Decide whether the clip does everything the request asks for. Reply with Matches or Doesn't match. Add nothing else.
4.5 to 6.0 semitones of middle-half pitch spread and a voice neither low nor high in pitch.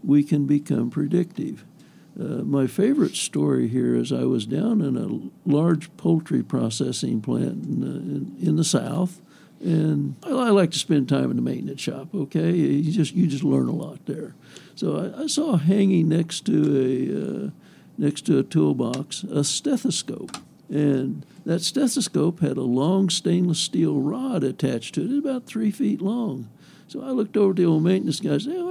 Matches